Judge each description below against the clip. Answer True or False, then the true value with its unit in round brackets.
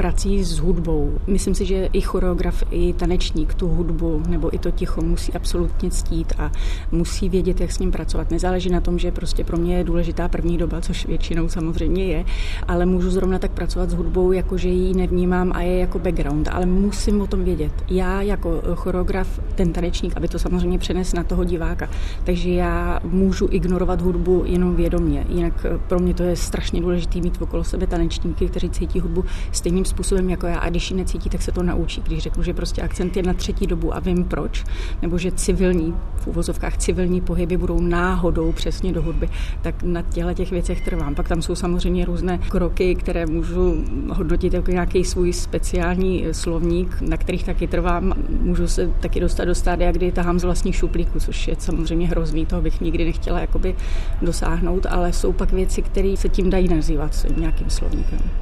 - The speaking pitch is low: False (175 Hz)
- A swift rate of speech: True (190 wpm)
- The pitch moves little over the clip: True (1.8 semitones)